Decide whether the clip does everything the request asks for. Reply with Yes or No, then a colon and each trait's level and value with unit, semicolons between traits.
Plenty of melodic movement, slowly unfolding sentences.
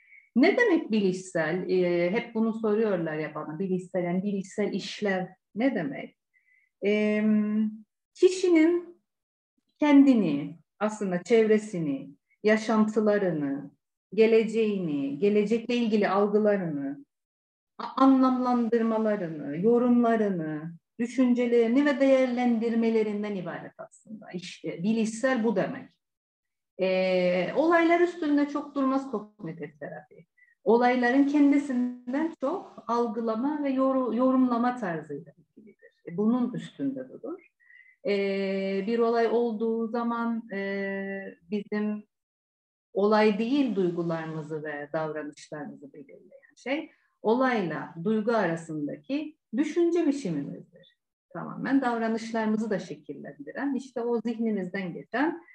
Yes: wide, 5.7 semitones; slow, 90 wpm